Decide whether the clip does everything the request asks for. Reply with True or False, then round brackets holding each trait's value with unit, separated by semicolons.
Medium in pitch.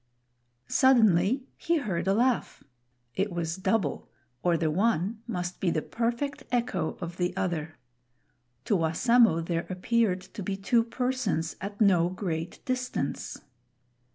False (195 Hz)